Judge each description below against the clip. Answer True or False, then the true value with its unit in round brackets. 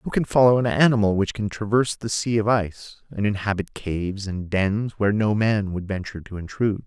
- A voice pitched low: True (105 Hz)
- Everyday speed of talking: False (210 wpm)